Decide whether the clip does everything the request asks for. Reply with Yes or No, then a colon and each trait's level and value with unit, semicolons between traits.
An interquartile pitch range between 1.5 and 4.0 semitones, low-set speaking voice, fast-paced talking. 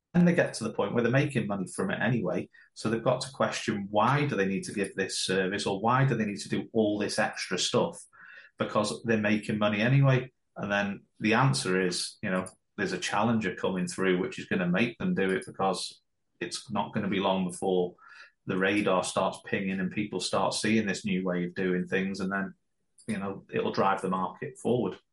Yes: average, 3.0 semitones; low, 100 Hz; fast, 220 wpm